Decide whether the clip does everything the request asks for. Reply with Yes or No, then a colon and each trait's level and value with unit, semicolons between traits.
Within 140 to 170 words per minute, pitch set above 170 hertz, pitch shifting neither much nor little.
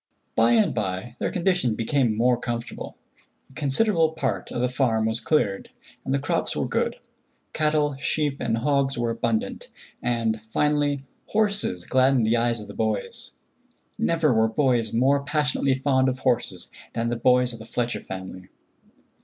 No: average, 160 wpm; low, 125 Hz; average, 3.8 semitones